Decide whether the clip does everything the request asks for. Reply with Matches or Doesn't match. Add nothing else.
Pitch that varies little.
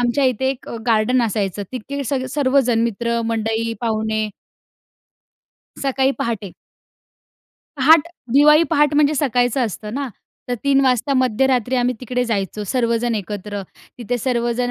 Doesn't match